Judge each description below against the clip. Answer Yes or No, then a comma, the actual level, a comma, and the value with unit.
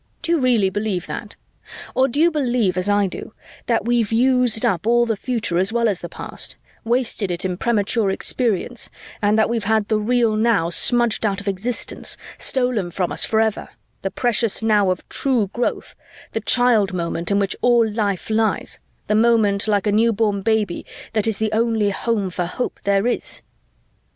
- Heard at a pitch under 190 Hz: No, high, 220 Hz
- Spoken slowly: No, average, 180 wpm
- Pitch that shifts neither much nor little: Yes, average, 3.0 semitones